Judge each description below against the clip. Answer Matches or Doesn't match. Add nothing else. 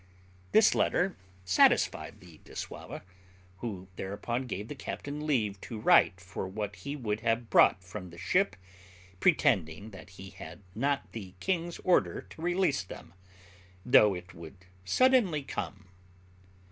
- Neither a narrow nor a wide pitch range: Doesn't match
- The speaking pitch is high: Doesn't match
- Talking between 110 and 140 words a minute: Matches